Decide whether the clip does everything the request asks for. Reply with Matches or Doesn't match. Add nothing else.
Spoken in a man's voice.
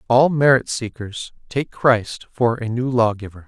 Matches